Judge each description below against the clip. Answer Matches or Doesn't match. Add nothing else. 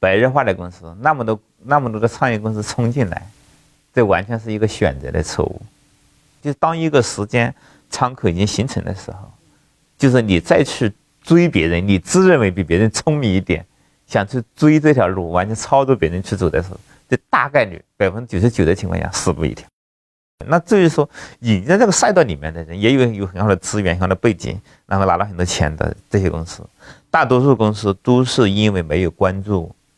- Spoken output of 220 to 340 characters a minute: Matches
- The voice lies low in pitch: Matches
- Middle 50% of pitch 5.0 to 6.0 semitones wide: Matches